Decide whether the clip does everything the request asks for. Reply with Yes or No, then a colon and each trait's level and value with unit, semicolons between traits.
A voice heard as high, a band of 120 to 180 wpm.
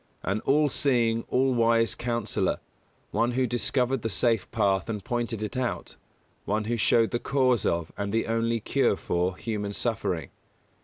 No: low, 115 Hz; average, 160 wpm